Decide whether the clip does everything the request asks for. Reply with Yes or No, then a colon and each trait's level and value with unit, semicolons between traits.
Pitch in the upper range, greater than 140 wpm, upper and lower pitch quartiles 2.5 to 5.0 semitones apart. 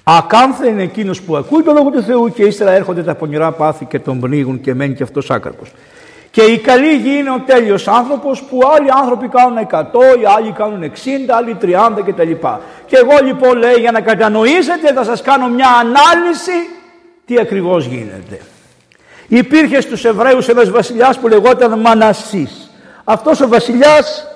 No: high, 235 Hz; fast, 170 wpm; wide, 5.4 semitones